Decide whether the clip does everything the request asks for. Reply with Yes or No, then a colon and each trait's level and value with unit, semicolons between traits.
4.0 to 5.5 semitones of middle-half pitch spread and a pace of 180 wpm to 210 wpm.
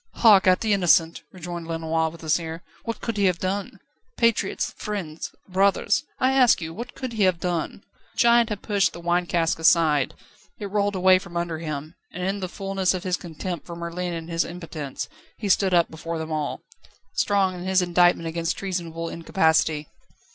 No: average, 2.9 semitones; average, 190 wpm